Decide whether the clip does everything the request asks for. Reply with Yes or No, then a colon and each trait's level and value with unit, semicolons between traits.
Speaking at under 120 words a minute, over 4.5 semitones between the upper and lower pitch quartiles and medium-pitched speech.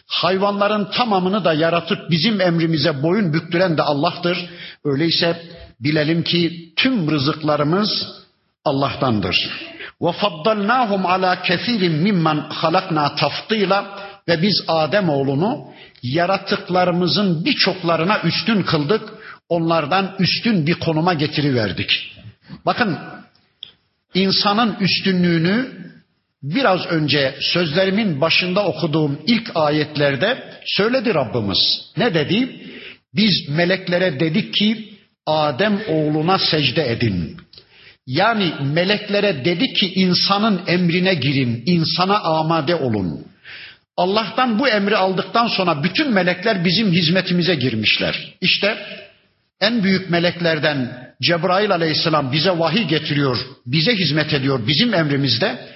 No: average, 100 wpm; average, 4.2 semitones; medium, 175 Hz